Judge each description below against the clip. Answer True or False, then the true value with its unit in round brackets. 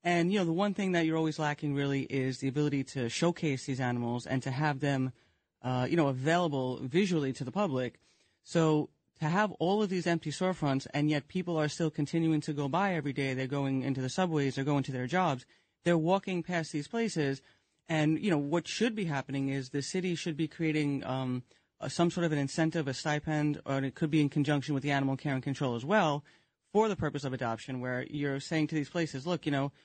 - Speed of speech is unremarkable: False (230 wpm)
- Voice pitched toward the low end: False (150 Hz)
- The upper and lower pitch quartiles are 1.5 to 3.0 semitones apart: False (3.8 semitones)